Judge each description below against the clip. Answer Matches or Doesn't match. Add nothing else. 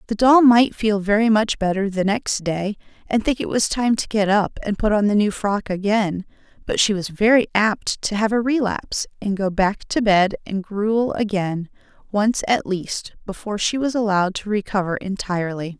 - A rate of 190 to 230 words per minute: Matches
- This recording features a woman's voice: Matches